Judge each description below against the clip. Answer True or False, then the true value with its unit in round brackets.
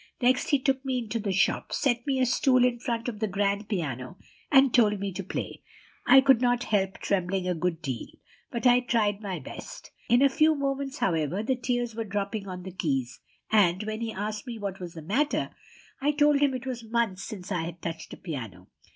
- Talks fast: True (215 wpm)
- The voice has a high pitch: True (215 Hz)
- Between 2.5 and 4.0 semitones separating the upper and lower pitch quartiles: False (5.2 semitones)